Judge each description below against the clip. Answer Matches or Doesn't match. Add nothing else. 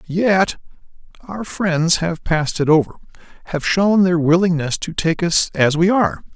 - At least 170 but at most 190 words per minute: Doesn't match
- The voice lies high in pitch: Doesn't match